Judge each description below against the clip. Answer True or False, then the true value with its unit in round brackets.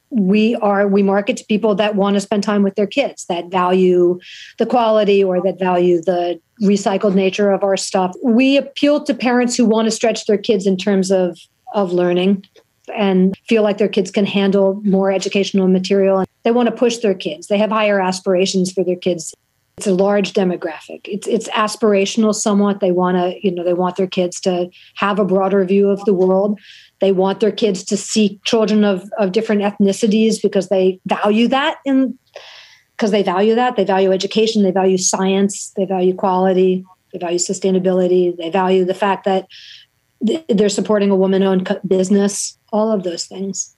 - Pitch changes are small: True (2.2 semitones)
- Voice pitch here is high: True (200 Hz)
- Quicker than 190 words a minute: False (185 wpm)